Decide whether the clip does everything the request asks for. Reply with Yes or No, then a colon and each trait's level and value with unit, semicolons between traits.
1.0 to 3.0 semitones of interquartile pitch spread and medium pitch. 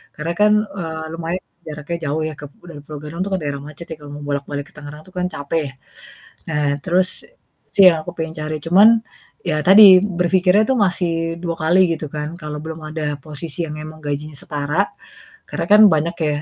Yes: narrow, 2.5 semitones; medium, 160 Hz